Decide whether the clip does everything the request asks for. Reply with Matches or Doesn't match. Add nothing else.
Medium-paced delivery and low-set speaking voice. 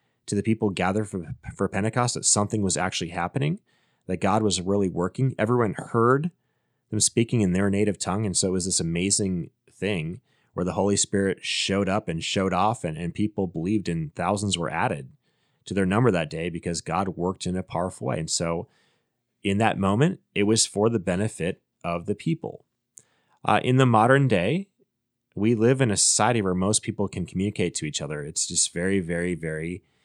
Matches